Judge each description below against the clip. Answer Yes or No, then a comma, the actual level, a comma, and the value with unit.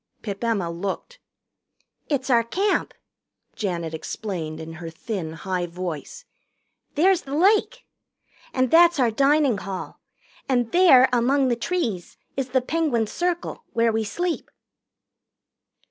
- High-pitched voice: Yes, high, 240 Hz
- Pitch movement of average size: No, wide, 8.9 semitones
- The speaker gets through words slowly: Yes, slow, 125 wpm